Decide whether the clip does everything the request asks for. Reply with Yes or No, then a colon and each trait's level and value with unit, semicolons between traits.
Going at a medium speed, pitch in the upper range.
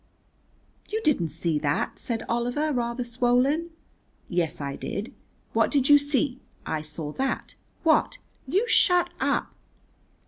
No: slow, 130 wpm; high, 245 Hz